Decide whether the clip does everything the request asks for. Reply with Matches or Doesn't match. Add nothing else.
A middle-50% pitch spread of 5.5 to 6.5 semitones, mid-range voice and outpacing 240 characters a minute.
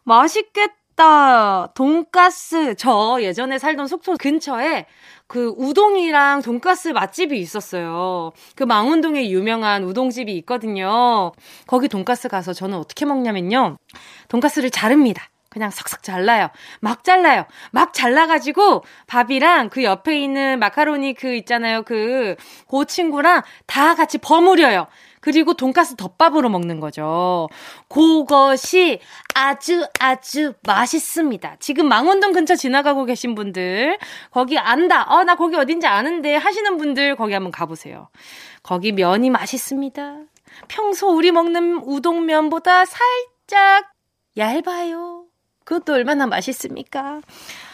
Doesn't match